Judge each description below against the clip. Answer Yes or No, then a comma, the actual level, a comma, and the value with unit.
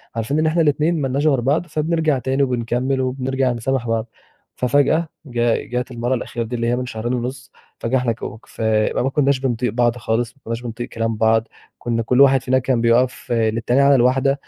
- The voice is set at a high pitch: No, low, 125 Hz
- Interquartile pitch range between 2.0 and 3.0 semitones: Yes, narrow, 2.5 semitones